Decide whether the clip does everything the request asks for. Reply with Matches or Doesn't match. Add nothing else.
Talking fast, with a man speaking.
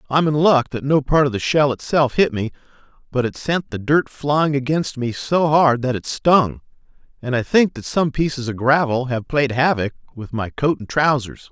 Matches